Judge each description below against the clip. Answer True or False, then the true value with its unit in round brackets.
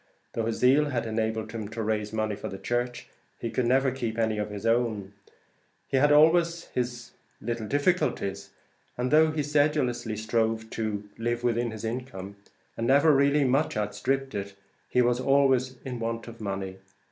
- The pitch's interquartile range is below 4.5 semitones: True (3.5 semitones)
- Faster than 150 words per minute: True (170 wpm)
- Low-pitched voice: True (120 Hz)